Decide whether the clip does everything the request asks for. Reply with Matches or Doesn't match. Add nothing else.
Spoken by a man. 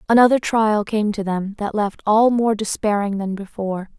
Doesn't match